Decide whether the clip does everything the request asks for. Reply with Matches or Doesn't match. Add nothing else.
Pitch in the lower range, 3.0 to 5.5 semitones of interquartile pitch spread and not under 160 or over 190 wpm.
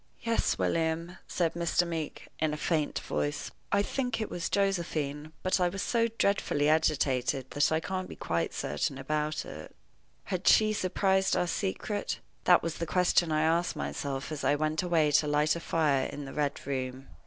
Doesn't match